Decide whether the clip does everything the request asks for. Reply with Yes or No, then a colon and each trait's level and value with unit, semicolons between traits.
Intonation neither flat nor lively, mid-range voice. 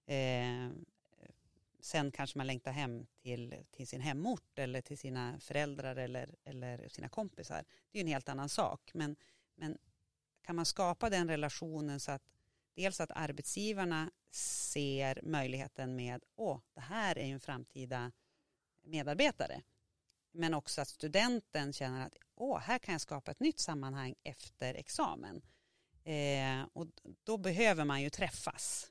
Yes: average, 4.0 semitones; medium, 145 Hz